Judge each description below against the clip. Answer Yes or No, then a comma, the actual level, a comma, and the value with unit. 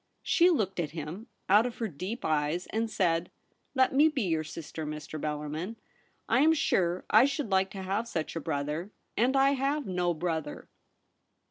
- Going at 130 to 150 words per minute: No, average, 180 wpm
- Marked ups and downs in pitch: Yes, wide, 7.2 semitones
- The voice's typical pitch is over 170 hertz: Yes, medium, 185 Hz